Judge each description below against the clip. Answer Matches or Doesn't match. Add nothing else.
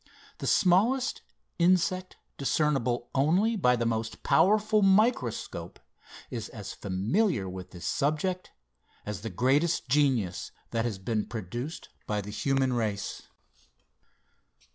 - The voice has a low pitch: Matches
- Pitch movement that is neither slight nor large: Doesn't match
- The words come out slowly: Matches